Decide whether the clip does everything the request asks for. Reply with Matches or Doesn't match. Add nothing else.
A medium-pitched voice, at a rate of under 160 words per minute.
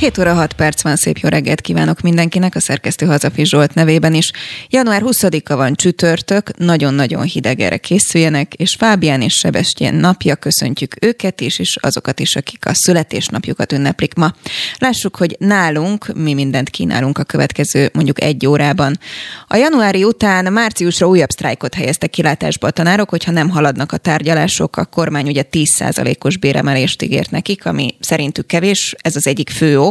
Doesn't match